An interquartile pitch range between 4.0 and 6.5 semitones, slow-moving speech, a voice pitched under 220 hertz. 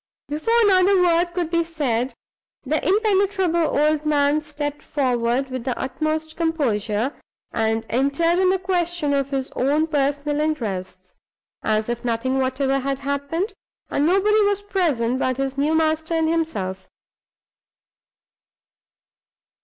No: average, 4.4 semitones; slow, 130 wpm; very high, 295 Hz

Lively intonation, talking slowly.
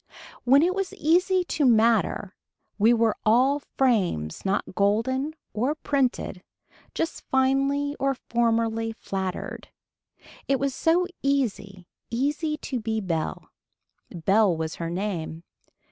Yes: wide, 5.7 semitones; slow, 115 wpm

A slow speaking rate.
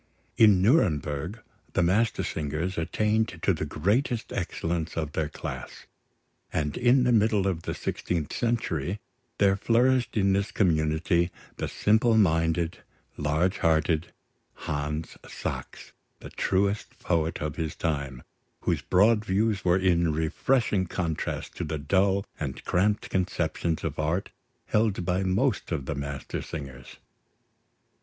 Yes: slow, 125 wpm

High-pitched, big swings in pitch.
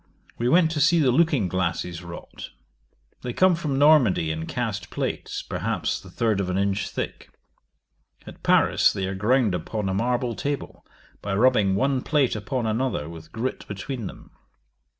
No: low, 115 Hz; wide, 5.7 semitones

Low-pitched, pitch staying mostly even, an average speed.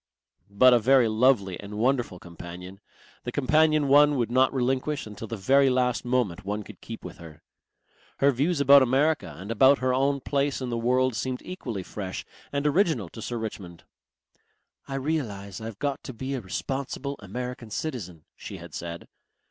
No: low, 125 Hz; average, 4.9 semitones; average, 170 wpm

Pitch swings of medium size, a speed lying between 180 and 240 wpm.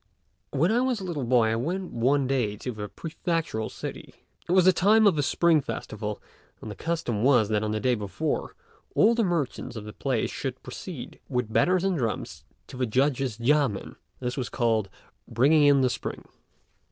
No: wide, 6.7 semitones; average, 190 wpm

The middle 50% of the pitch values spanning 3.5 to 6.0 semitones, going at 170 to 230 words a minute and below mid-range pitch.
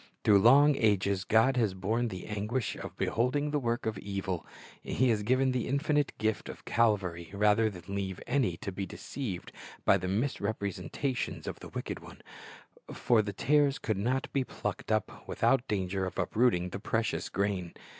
Yes: average, 4.5 semitones; average, 175 wpm; low, 110 Hz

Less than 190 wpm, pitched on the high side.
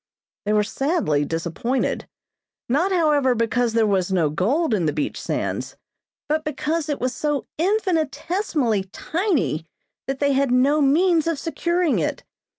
Yes: average, 145 wpm; very high, 275 Hz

